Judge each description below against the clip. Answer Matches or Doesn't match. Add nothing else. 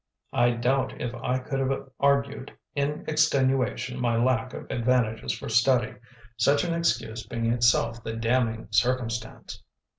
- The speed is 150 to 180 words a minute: Doesn't match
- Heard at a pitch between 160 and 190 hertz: Doesn't match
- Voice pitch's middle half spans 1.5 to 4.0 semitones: Matches